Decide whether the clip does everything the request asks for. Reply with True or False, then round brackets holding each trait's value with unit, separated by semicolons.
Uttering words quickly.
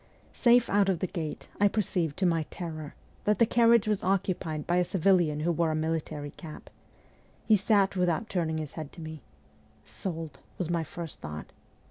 False (190 wpm)